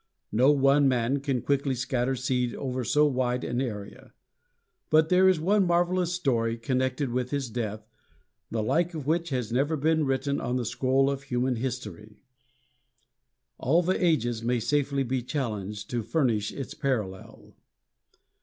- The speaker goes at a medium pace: Yes, average, 155 wpm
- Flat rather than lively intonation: No, average, 3.4 semitones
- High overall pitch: No, low, 130 Hz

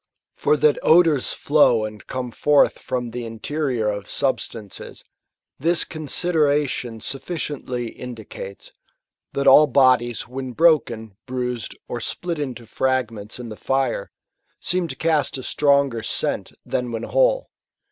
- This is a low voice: Yes, low, 130 Hz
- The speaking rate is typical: No, slow, 125 wpm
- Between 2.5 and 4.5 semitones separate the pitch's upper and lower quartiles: Yes, average, 4.2 semitones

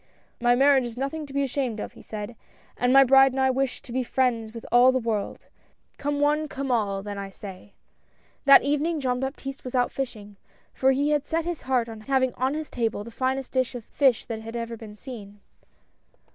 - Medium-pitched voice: No, very high, 255 Hz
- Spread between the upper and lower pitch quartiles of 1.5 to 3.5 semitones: Yes, average, 3.2 semitones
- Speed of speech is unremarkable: No, fast, 225 wpm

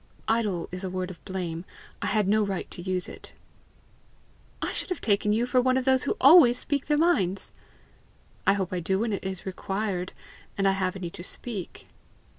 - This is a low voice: No, high, 195 Hz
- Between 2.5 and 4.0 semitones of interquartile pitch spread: No, average, 4.5 semitones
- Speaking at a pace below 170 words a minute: No, average, 200 wpm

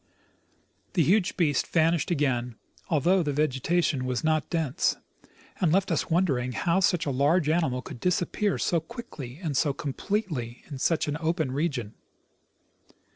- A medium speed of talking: Yes, average, 150 wpm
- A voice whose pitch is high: No, medium, 155 Hz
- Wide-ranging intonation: No, average, 4.6 semitones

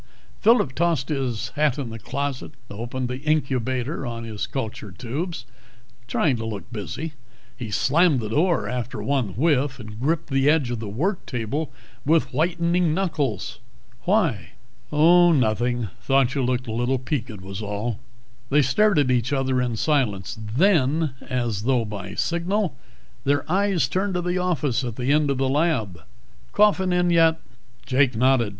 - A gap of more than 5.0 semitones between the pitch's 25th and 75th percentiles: Yes, wide, 5.5 semitones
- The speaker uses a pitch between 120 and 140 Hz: Yes, low, 135 Hz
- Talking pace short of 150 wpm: No, average, 160 wpm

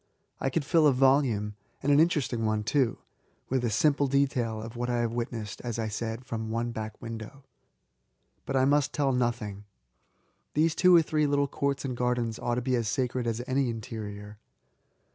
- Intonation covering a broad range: No, average, 3.5 semitones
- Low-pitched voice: Yes, low, 120 Hz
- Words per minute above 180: Yes, average, 200 wpm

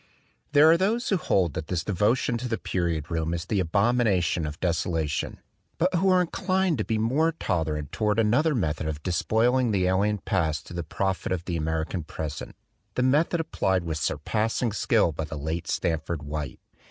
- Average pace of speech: Yes, average, 185 wpm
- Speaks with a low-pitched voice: Yes, very low, 95 Hz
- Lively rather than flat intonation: Yes, wide, 7.3 semitones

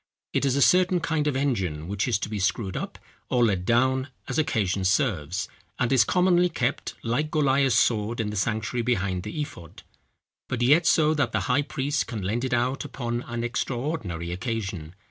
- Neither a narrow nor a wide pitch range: No, wide, 5.7 semitones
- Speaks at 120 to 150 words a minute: No, average, 185 wpm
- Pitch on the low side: Yes, low, 120 Hz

